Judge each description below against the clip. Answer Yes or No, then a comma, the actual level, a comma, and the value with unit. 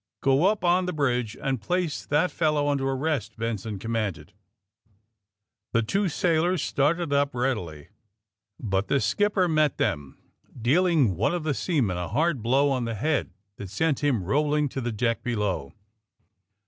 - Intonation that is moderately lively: No, wide, 5.8 semitones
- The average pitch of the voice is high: No, low, 135 Hz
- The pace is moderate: Yes, average, 155 wpm